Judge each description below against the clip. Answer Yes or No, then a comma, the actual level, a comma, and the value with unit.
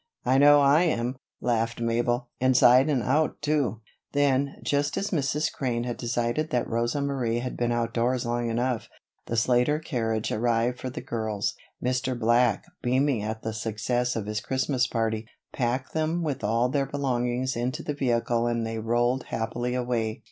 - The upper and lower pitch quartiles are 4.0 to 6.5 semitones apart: No, narrow, 2.5 semitones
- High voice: No, low, 120 Hz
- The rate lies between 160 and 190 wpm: Yes, average, 165 wpm